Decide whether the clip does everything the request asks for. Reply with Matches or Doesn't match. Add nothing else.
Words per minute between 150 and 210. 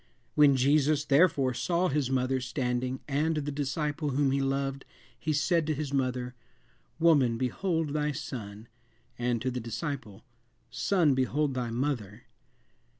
Doesn't match